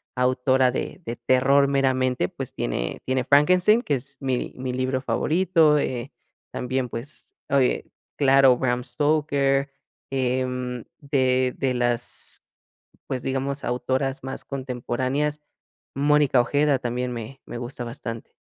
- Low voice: Yes, low, 130 Hz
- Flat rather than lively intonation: Yes, narrow, 1.9 semitones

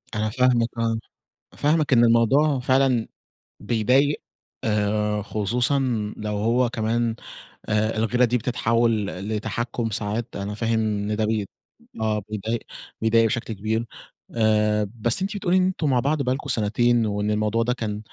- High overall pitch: No, low, 115 Hz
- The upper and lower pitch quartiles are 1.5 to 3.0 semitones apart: Yes, narrow, 2.5 semitones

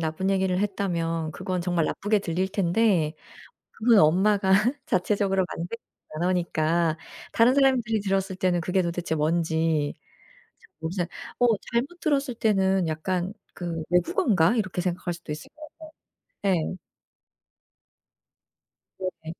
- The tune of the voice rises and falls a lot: No, average, 3.3 semitones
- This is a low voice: No, medium, 185 Hz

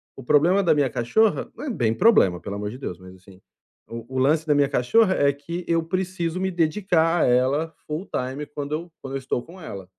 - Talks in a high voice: No, medium, 150 Hz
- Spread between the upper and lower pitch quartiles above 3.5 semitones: Yes, wide, 5.6 semitones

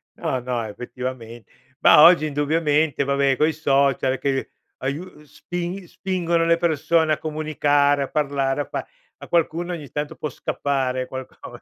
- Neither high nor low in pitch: Yes, medium, 145 Hz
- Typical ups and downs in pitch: Yes, average, 3.3 semitones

